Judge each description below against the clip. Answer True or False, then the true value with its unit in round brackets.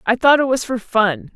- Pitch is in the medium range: False (240 Hz)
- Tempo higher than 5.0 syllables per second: False (4.9 syllables/s)